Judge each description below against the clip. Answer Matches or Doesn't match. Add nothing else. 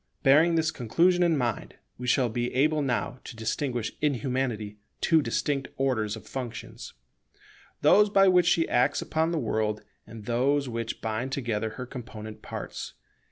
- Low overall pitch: Matches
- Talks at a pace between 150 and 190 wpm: Matches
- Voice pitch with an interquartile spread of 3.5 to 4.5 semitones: Doesn't match